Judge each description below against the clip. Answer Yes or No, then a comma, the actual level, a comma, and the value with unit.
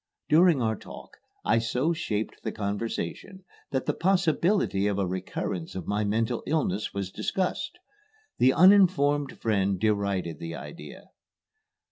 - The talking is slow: Yes, slow, 130 wpm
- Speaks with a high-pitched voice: No, low, 110 Hz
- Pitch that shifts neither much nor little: No, wide, 8.2 semitones